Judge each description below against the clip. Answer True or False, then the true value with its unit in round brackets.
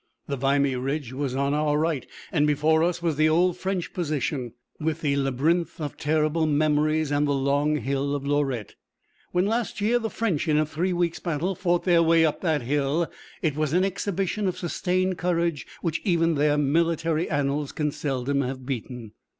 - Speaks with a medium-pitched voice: True (155 Hz)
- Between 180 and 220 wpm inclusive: True (185 wpm)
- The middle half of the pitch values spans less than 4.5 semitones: True (3.2 semitones)